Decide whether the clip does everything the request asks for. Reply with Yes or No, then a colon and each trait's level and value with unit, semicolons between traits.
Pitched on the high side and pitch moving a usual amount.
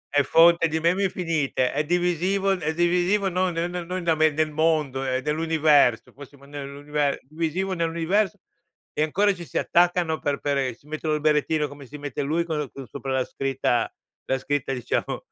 No: medium, 155 Hz; average, 3.3 semitones